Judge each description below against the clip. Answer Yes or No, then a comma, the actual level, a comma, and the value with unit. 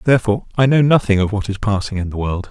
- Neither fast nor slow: No, fast, 265 wpm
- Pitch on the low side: Yes, low, 110 Hz